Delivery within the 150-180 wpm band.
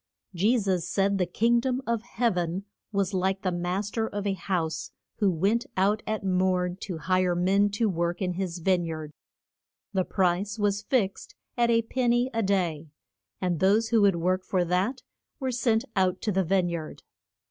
No: average, 190 wpm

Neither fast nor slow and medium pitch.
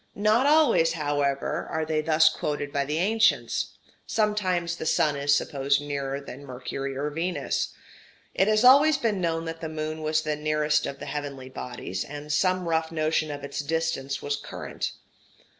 Yes: average, 170 wpm; medium, 155 Hz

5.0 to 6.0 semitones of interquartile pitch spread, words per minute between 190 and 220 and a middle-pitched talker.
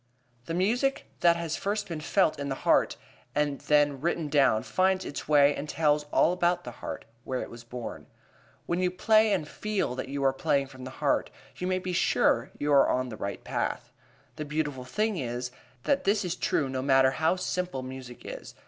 Yes: wide, 5.4 semitones; average, 200 wpm; medium, 150 Hz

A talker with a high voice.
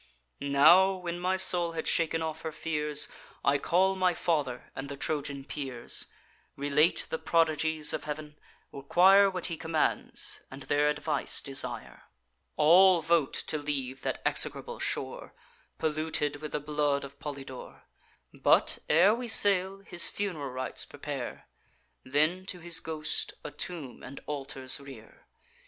No: medium, 155 Hz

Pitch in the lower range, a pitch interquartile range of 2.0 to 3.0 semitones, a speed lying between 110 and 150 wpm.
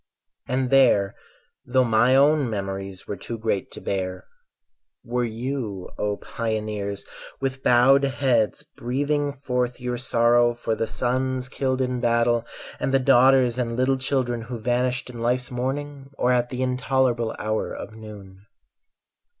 Yes: low, 125 Hz; average, 2.7 semitones; average, 140 wpm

